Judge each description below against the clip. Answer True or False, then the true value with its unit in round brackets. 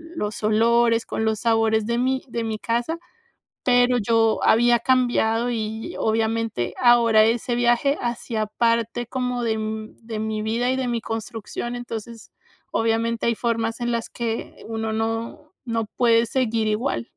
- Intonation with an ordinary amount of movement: False (1.4 semitones)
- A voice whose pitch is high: True (230 Hz)